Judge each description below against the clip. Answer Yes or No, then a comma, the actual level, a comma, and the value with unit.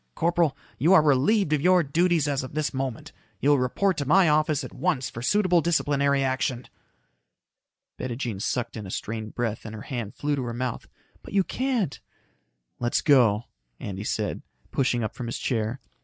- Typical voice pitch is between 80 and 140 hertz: Yes, low, 135 Hz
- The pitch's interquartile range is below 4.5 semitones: No, average, 5.0 semitones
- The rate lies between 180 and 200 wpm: Yes, average, 185 wpm